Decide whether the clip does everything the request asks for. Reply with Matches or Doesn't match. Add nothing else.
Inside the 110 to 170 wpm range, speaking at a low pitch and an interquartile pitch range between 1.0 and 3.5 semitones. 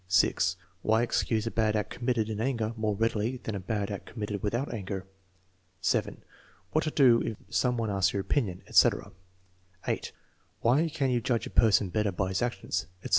Doesn't match